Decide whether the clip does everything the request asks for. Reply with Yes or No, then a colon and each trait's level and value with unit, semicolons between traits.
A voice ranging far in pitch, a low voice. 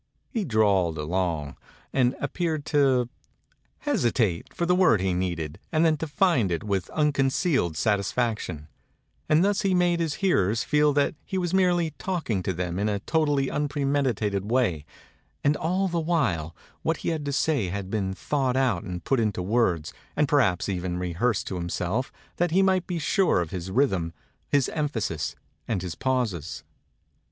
Yes: wide, 9.0 semitones; low, 120 Hz